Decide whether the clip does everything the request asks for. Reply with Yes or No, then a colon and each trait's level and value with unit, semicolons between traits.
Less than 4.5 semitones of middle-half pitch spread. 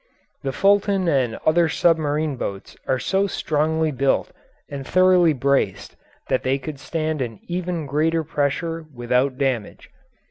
Yes: average, 3.6 semitones